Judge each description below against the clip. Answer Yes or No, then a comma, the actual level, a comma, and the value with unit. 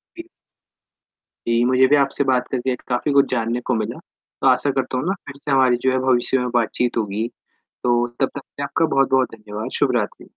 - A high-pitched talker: No, low, 130 Hz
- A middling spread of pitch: No, narrow, 2.0 semitones